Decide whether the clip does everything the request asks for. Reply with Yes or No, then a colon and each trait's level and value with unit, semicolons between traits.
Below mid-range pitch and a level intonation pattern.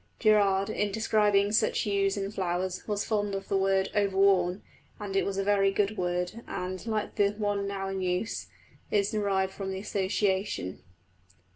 No: high, 195 Hz; narrow, 1.3 semitones